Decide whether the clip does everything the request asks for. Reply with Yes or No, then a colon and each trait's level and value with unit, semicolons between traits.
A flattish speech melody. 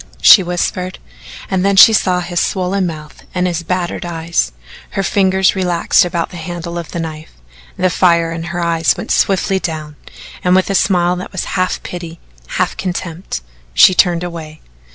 Yes: narrow, 1.7 semitones